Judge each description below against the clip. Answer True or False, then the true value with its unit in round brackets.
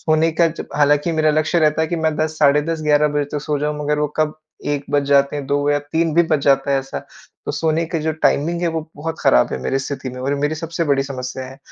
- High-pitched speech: False (150 Hz)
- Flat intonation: True (1.9 semitones)